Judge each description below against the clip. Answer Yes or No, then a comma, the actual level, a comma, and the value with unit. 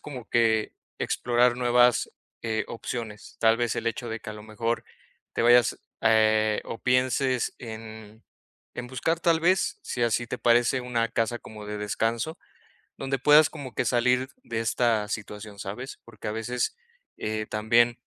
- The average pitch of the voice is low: Yes, low, 115 Hz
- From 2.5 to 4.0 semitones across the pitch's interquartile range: No, narrow, 2.1 semitones